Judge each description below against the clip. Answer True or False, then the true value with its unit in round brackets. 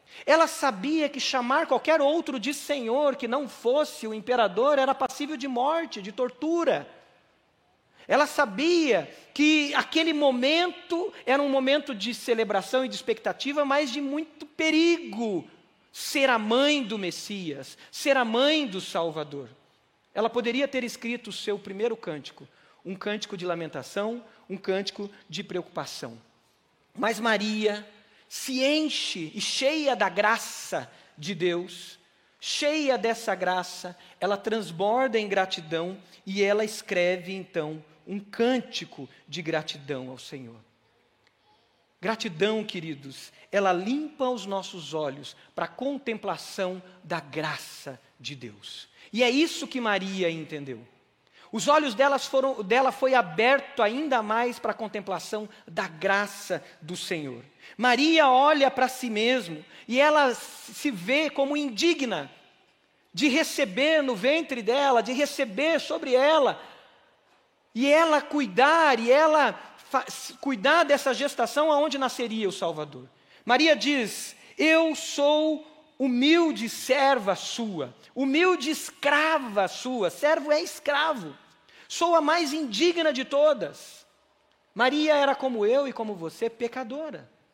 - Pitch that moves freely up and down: True (6.9 semitones)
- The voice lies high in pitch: True (245 Hz)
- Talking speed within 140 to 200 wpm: False (125 wpm)